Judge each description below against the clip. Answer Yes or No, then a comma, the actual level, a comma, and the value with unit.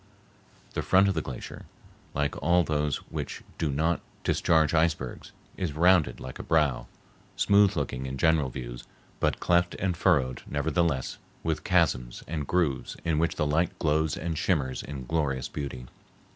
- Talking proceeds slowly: No, average, 155 wpm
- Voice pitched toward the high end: No, very low, 75 Hz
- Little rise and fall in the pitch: No, average, 3.8 semitones